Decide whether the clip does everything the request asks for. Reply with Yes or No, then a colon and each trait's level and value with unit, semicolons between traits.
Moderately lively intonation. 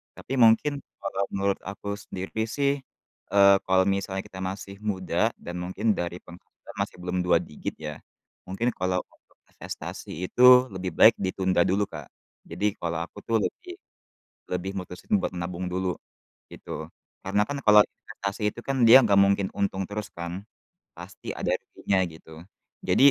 No: narrow, 2.0 semitones